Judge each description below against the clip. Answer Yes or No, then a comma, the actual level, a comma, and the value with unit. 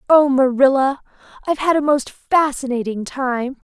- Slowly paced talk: Yes, slow, 130 wpm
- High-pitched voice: Yes, very high, 270 Hz